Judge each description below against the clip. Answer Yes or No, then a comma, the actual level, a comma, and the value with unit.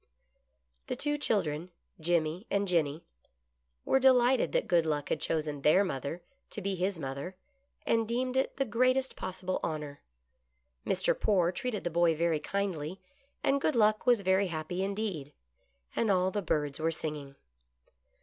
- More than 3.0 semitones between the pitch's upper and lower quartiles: Yes, wide, 5.5 semitones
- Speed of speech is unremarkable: Yes, average, 160 wpm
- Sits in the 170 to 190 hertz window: Yes, medium, 185 Hz